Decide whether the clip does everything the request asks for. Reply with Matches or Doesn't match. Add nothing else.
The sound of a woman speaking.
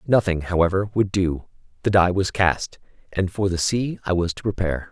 Doesn't match